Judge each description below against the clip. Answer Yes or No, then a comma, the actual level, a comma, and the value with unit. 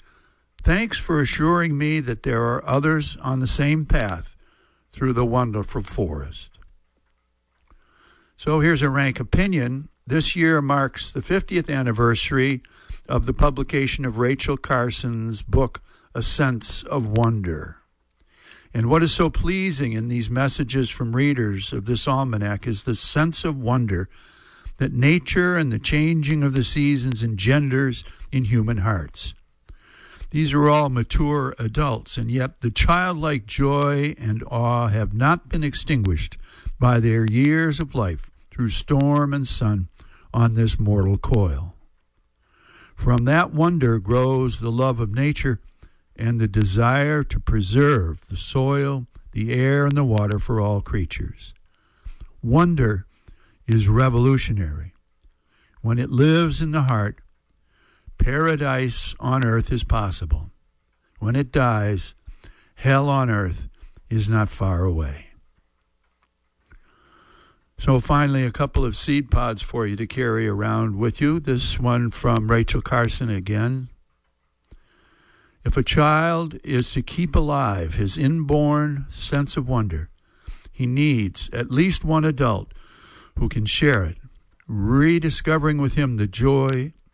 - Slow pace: Yes, slow, 130 wpm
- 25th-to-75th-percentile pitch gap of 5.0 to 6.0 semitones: Yes, wide, 5.5 semitones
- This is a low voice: Yes, low, 120 Hz